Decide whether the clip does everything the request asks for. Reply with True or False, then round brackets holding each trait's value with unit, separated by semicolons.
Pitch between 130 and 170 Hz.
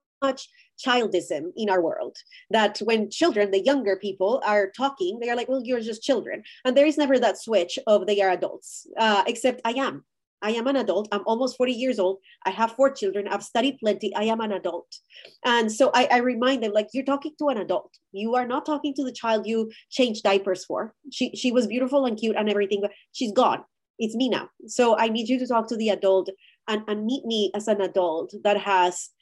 False (230 Hz)